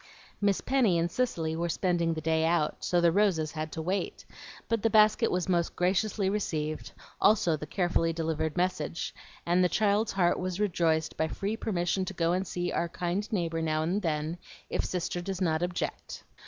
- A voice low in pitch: No, medium, 175 Hz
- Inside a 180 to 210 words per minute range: Yes, average, 185 wpm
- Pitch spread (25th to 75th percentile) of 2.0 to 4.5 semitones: Yes, average, 3.0 semitones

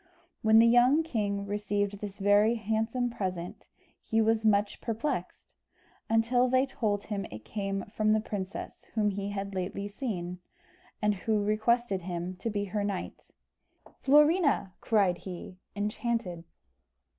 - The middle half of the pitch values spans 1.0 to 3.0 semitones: Yes, narrow, 2.4 semitones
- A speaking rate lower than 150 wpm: Yes, slow, 135 wpm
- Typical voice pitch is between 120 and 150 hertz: No, high, 210 Hz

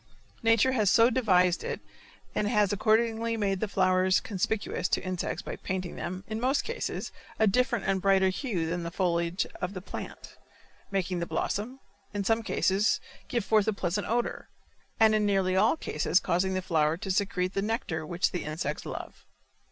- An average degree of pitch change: Yes, average, 3.3 semitones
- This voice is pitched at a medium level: No, high, 195 Hz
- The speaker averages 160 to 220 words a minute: Yes, average, 175 wpm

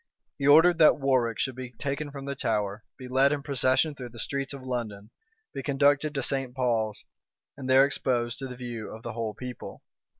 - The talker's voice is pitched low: Yes, low, 130 Hz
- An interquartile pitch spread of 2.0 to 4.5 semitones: Yes, average, 2.8 semitones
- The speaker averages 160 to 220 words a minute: Yes, average, 200 wpm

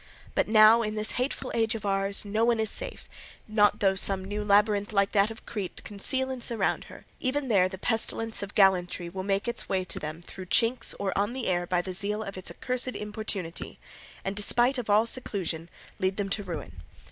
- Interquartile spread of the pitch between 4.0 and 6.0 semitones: No, average, 2.8 semitones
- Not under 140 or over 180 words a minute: No, fast, 205 wpm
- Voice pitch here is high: Yes, high, 205 Hz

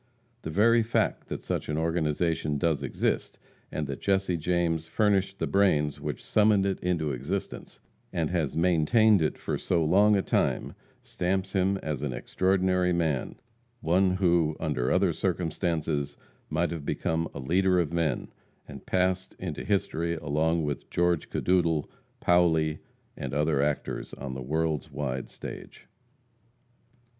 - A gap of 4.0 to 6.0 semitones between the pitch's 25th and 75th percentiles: No, average, 3.5 semitones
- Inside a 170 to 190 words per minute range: No, average, 145 wpm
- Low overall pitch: Yes, very low, 85 Hz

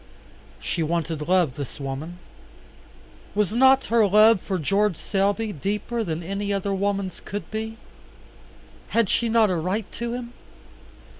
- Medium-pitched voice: No, high, 200 Hz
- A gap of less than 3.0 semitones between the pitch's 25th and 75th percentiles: No, average, 4.2 semitones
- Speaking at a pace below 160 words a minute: Yes, average, 140 wpm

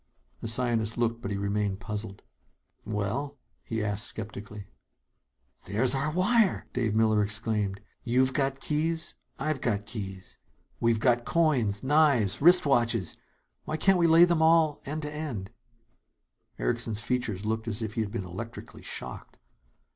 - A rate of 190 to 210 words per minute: No, average, 145 wpm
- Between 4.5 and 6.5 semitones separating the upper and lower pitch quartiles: Yes, wide, 5.6 semitones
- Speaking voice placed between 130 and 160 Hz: No, low, 115 Hz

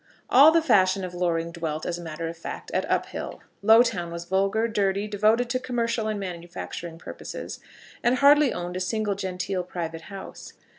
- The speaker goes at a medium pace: Yes, average, 170 wpm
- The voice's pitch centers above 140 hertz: Yes, high, 190 Hz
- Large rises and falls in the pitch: No, average, 4.4 semitones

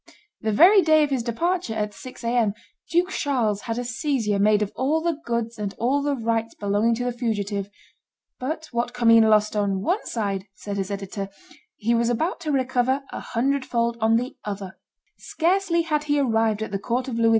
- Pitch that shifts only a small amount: No, average, 4.6 semitones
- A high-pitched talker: Yes, high, 235 Hz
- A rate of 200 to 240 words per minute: Yes, fast, 205 wpm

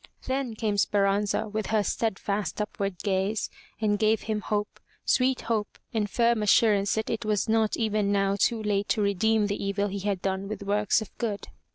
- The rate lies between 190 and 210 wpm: Yes, average, 195 wpm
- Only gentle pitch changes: Yes, narrow, 1.6 semitones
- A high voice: Yes, high, 210 Hz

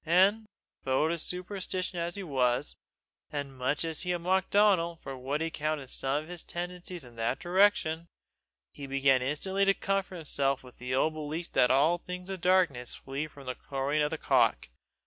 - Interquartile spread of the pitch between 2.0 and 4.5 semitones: No, average, 4.9 semitones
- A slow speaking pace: No, average, 195 wpm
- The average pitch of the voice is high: No, medium, 160 Hz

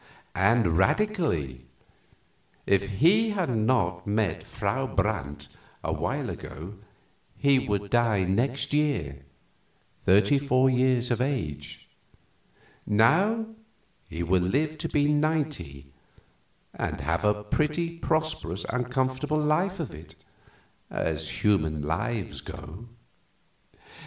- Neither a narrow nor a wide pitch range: No, wide, 8.4 semitones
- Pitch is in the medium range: No, low, 115 Hz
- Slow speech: Yes, slow, 105 wpm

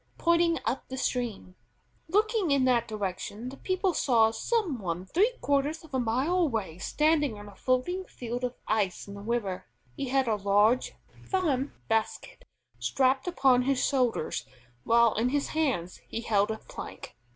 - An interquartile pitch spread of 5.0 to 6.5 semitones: Yes, wide, 5.5 semitones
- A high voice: Yes, very high, 255 Hz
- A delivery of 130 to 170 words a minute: Yes, average, 165 wpm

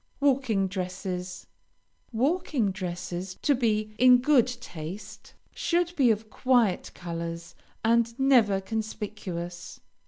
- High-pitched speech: Yes, high, 215 Hz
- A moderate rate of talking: No, slow, 100 wpm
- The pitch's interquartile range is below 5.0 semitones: No, wide, 5.4 semitones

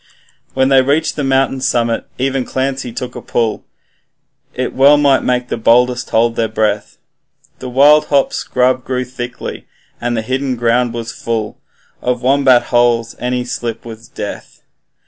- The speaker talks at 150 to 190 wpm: Yes, average, 160 wpm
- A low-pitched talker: Yes, low, 125 Hz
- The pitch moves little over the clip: Yes, narrow, 2.0 semitones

